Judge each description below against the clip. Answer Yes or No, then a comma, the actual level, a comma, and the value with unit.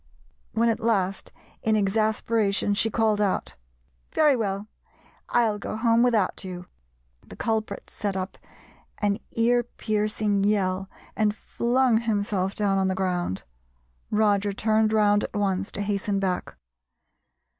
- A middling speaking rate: No, slow, 130 wpm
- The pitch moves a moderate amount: No, narrow, 2.1 semitones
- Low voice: No, high, 210 Hz